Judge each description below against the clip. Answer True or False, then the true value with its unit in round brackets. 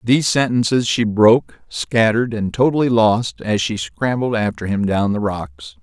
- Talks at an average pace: True (165 wpm)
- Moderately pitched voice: False (115 Hz)